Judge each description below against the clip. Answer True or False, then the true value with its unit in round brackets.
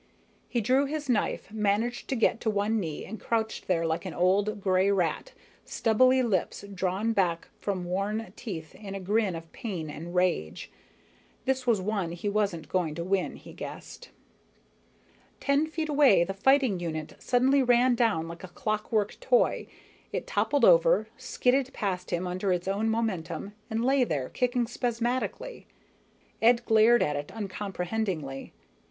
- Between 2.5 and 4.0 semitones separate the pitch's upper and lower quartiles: False (5.0 semitones)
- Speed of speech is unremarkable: True (155 wpm)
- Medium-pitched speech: False (205 Hz)